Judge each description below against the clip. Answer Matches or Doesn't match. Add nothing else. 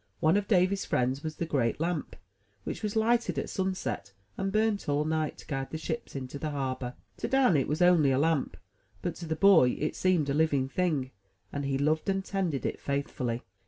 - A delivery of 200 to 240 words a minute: Matches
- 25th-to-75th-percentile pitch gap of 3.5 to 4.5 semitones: Doesn't match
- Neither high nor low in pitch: Matches